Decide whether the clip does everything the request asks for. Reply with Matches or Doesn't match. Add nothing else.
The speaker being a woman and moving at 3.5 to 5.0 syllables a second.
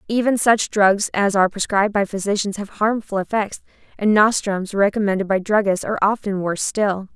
Doesn't match